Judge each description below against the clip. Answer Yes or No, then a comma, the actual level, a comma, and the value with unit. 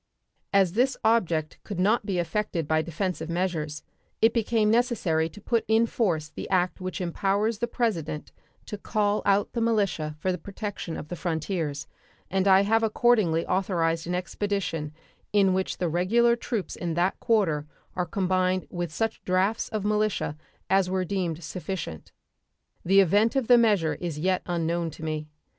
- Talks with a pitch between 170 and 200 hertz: Yes, medium, 185 Hz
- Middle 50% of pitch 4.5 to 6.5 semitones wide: No, average, 4.1 semitones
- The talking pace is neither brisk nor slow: Yes, average, 165 wpm